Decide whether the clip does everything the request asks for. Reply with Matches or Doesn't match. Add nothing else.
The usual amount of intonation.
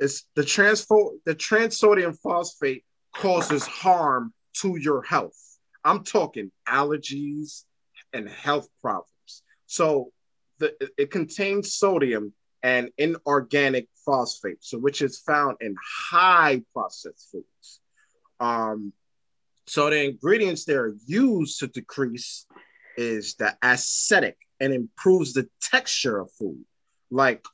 Doesn't match